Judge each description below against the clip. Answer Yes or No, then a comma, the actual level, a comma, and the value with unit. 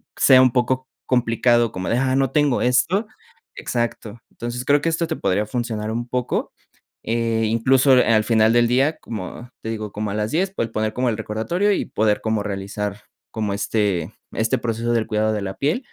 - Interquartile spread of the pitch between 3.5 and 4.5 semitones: No, average, 3.1 semitones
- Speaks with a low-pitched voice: Yes, low, 115 Hz